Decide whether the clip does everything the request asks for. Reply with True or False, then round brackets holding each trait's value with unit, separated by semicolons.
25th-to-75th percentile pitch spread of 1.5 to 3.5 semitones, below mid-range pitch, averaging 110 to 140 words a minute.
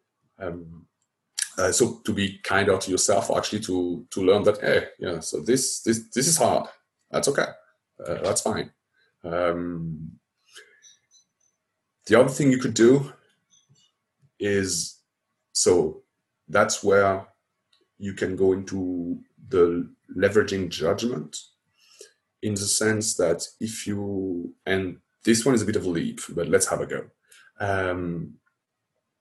False (4.0 semitones; 95 Hz; 135 wpm)